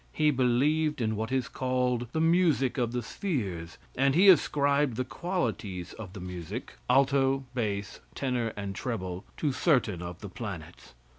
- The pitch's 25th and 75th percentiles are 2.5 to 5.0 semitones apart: No, wide, 5.5 semitones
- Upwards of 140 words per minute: Yes, average, 155 wpm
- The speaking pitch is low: Yes, low, 125 Hz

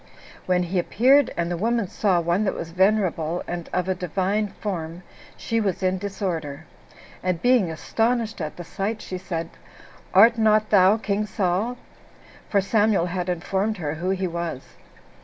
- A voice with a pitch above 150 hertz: Yes, high, 190 Hz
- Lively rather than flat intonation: No, average, 3.6 semitones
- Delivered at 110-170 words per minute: Yes, average, 160 wpm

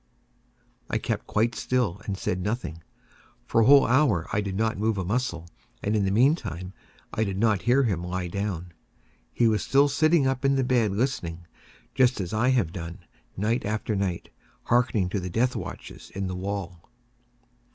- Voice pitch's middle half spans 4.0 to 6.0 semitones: Yes, average, 5.1 semitones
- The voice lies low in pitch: Yes, low, 105 Hz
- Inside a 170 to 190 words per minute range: Yes, average, 175 wpm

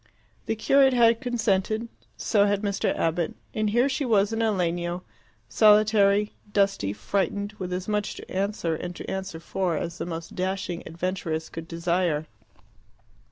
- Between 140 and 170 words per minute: Yes, average, 155 wpm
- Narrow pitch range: No, average, 3.6 semitones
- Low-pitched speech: No, high, 195 Hz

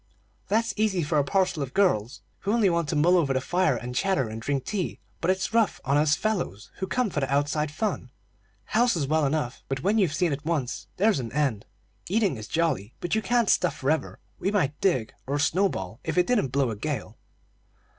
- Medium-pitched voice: Yes, medium, 155 Hz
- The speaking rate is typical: No, fast, 215 wpm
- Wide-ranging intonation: Yes, wide, 6.1 semitones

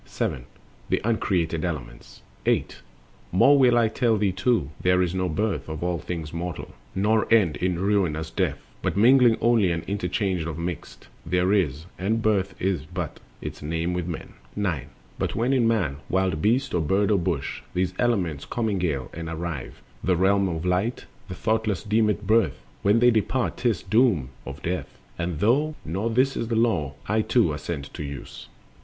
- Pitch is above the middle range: No, very low, 95 Hz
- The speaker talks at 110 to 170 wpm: No, average, 185 wpm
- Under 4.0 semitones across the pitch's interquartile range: No, average, 5.0 semitones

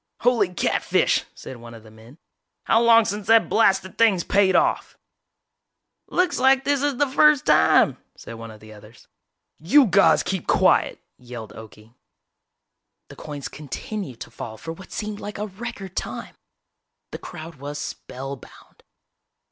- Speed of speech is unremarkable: Yes, average, 150 wpm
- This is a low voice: No, medium, 185 Hz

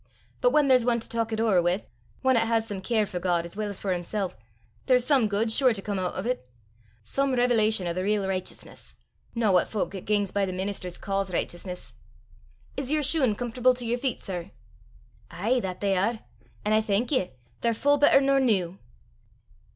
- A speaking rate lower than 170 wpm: No, fast, 205 wpm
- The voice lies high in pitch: Yes, high, 215 Hz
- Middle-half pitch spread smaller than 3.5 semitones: No, average, 4.5 semitones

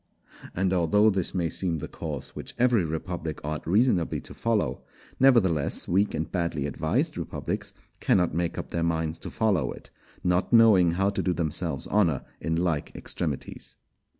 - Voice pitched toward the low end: Yes, very low, 85 Hz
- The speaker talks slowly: No, average, 160 wpm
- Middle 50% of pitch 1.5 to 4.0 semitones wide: Yes, average, 3.3 semitones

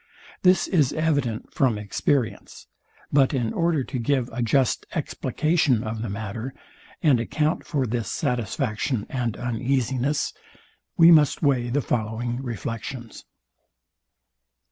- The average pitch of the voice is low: Yes, low, 125 Hz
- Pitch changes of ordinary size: Yes, average, 3.9 semitones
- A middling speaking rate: No, slow, 120 wpm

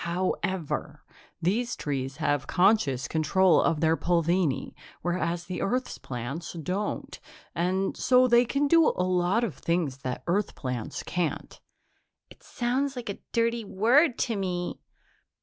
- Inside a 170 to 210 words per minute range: No, slow, 135 wpm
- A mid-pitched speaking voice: Yes, medium, 180 Hz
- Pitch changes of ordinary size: No, wide, 6.1 semitones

